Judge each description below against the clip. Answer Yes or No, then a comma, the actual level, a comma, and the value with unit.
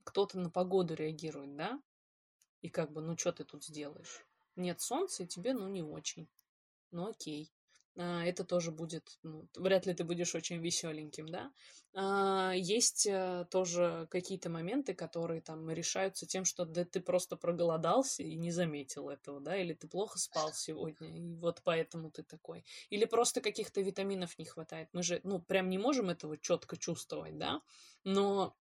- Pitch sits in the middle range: Yes, medium, 175 Hz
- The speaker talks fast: Yes, fast, 165 wpm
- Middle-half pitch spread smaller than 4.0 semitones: Yes, average, 2.8 semitones